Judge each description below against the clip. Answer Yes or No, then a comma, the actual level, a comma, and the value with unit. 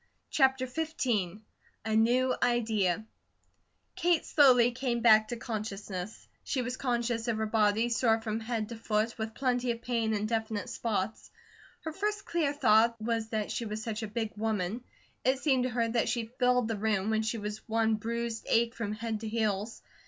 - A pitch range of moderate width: No, narrow, 2.1 semitones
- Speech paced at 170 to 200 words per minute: Yes, average, 180 wpm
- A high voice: Yes, high, 225 Hz